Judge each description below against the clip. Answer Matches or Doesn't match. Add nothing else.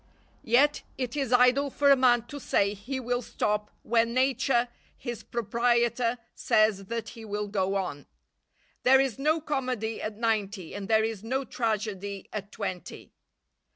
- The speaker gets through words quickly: Doesn't match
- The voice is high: Matches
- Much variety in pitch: Doesn't match